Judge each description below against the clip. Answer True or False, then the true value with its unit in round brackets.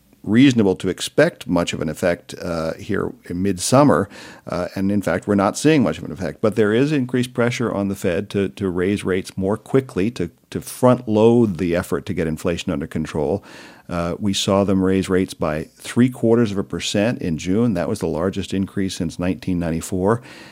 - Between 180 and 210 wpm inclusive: True (200 wpm)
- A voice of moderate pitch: False (95 Hz)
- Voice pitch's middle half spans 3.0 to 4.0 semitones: True (3.3 semitones)